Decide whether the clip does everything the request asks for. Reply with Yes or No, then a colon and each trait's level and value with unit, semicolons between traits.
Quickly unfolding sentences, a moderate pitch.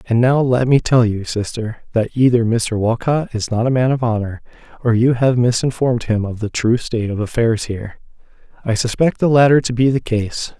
No: fast, 210 wpm; low, 120 Hz